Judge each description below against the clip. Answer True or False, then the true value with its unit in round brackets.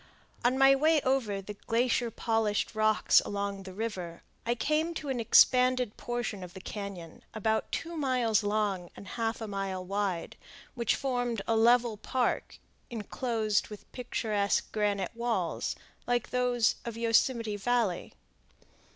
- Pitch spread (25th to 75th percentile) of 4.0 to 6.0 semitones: False (3.3 semitones)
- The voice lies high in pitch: True (225 Hz)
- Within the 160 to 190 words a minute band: False (140 wpm)